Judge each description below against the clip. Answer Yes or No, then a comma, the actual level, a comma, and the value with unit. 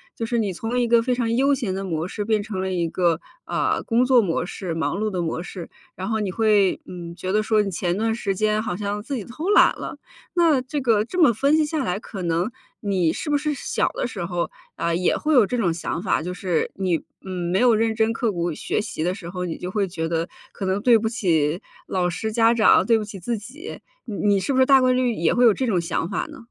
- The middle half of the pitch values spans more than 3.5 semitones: Yes, average, 4.7 semitones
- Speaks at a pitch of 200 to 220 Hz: Yes, high, 210 Hz